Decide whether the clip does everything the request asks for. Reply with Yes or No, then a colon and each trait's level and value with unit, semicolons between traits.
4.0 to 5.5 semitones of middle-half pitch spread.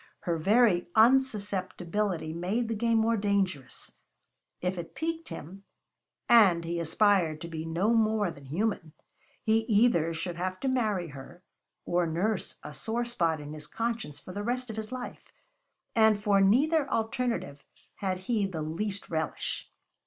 Yes: average, 5.0 semitones